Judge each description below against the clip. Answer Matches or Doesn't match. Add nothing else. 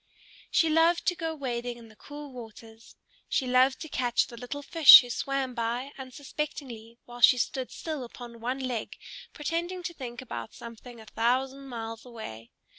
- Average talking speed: Matches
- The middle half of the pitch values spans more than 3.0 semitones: Matches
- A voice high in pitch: Matches